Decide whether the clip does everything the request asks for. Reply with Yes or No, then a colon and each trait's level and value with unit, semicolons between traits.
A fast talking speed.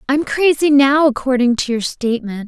No: average, 170 wpm